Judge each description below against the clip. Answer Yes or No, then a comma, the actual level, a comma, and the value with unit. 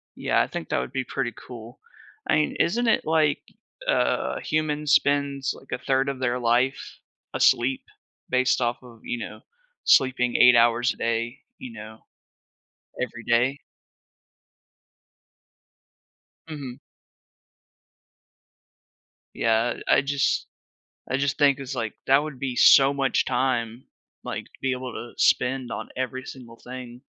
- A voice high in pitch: No, low, 130 Hz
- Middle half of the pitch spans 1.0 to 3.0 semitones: Yes, narrow, 2.5 semitones